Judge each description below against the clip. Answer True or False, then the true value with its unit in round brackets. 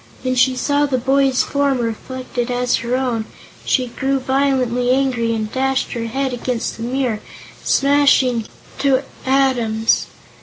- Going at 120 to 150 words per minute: True (145 wpm)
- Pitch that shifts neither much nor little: False (2.1 semitones)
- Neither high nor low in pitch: False (255 Hz)